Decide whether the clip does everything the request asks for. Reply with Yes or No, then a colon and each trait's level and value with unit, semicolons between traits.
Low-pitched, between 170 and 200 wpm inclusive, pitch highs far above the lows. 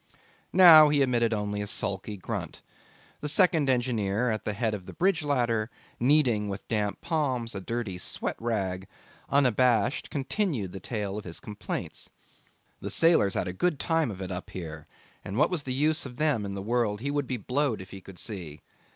Yes: low, 115 Hz; average, 190 wpm; wide, 6.1 semitones